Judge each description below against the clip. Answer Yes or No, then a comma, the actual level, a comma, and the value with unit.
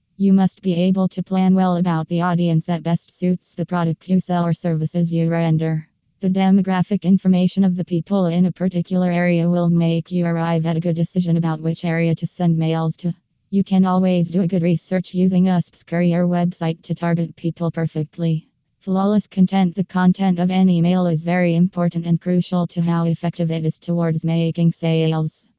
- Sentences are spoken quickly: No, average, 190 wpm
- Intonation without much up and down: Yes, narrow, 1.7 semitones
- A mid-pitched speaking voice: Yes, medium, 175 Hz